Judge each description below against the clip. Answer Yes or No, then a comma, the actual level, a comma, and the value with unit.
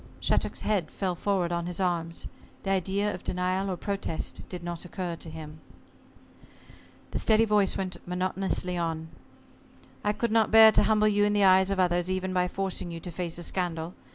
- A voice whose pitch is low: No, medium, 185 Hz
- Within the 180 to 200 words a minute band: Yes, average, 185 wpm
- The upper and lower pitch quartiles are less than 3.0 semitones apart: Yes, narrow, 2.4 semitones